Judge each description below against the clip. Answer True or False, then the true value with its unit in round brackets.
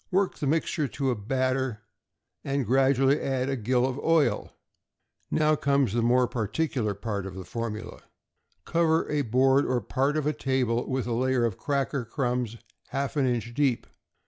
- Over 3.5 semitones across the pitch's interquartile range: False (3.0 semitones)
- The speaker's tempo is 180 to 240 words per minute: False (170 wpm)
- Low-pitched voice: True (130 Hz)